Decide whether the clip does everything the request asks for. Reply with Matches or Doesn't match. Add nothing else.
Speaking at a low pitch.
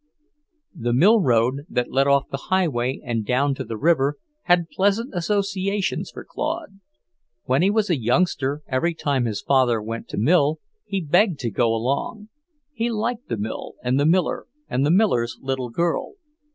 Doesn't match